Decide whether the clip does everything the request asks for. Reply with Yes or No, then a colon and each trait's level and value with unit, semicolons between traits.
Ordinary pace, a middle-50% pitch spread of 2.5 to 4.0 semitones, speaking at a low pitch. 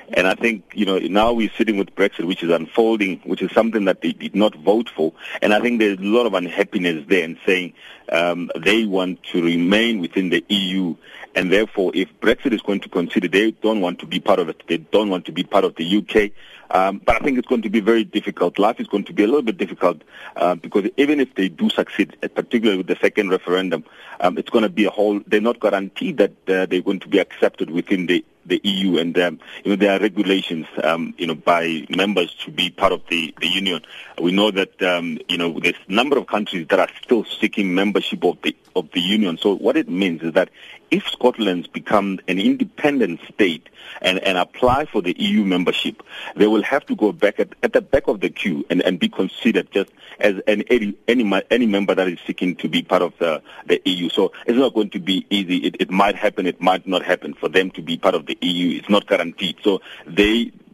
No: fast, 235 wpm; average, 3.2 semitones; low, 100 Hz